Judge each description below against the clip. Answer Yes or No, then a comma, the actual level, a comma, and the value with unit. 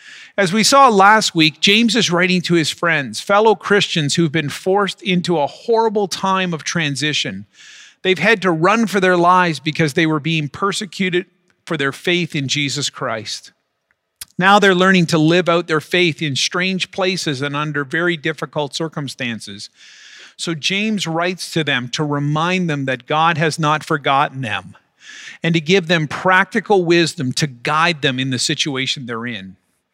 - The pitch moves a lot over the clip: No, average, 4.4 semitones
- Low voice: No, medium, 165 Hz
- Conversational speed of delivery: Yes, average, 170 wpm